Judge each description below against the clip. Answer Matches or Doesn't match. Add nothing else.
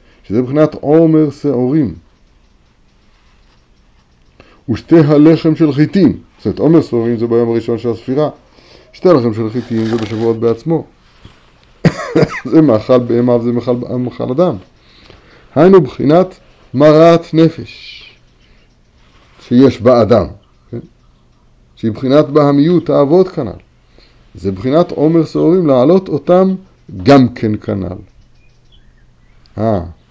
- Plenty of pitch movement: Matches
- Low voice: Matches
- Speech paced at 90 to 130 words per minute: Matches